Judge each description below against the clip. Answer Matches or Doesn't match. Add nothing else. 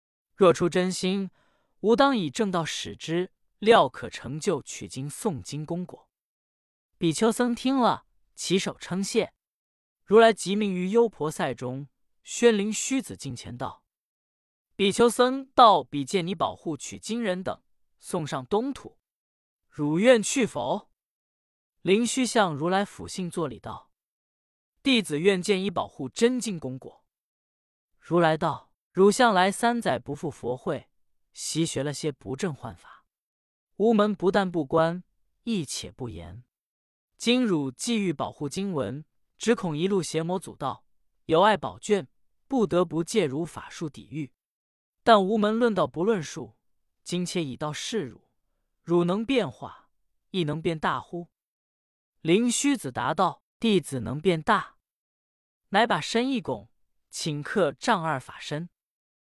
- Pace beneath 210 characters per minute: Matches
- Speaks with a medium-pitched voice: Matches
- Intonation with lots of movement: Matches